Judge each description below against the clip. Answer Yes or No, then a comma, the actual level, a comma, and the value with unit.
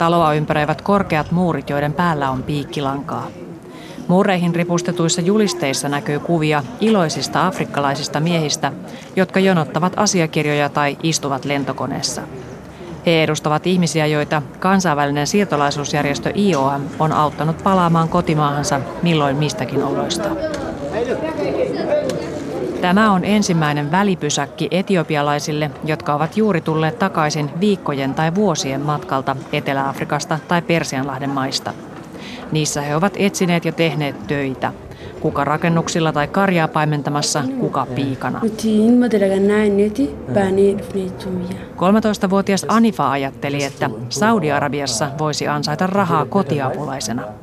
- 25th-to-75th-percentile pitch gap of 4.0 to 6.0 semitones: Yes, average, 4.3 semitones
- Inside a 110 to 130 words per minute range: No, slow, 95 wpm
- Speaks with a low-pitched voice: No, medium, 155 Hz